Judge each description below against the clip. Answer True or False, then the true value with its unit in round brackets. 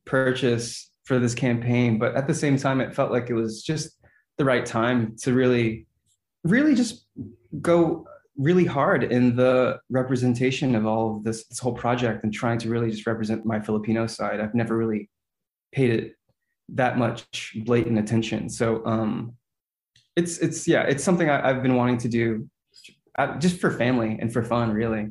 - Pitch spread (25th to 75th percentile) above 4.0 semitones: False (2.7 semitones)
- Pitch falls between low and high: False (120 Hz)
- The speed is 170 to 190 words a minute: True (175 wpm)